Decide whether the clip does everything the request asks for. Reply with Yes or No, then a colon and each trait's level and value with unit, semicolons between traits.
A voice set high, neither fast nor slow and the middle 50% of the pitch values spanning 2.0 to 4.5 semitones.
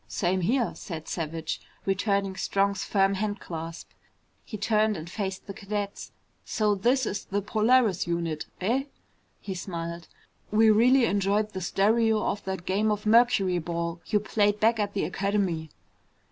Yes: high, 200 Hz; average, 145 wpm; average, 3.1 semitones